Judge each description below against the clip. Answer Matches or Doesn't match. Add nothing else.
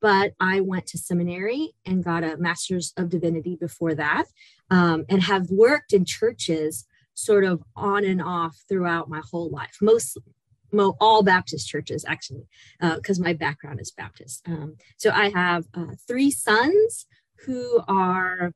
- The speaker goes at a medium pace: Matches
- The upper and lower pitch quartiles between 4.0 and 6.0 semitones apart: Doesn't match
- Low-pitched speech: Doesn't match